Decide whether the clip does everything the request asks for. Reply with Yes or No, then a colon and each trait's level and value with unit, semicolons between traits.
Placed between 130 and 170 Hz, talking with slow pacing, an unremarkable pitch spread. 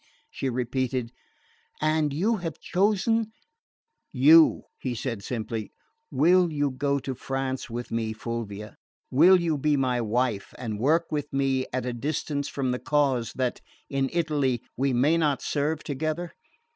No: low, 135 Hz; average, 150 wpm; average, 3.9 semitones